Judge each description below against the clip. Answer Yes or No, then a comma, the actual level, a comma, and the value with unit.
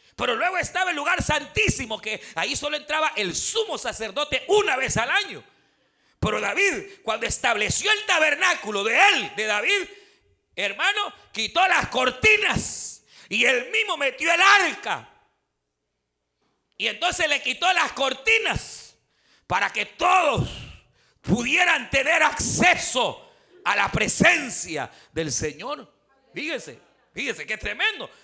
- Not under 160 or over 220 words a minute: No, slow, 125 wpm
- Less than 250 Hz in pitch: No, very high, 345 Hz